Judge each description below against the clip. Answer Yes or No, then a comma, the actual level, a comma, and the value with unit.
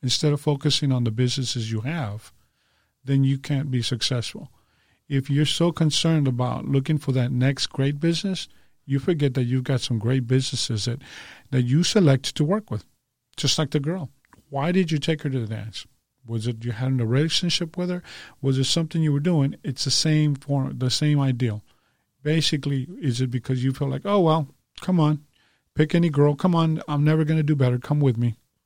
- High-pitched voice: No, medium, 140 Hz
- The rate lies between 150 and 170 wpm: No, fast, 205 wpm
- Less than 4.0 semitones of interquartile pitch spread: Yes, average, 3.4 semitones